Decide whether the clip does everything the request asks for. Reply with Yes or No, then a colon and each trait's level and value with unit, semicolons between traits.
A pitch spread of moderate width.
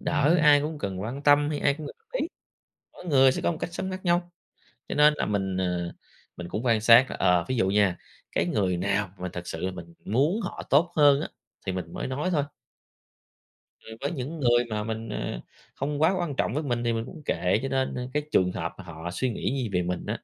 No: wide, 7.8 semitones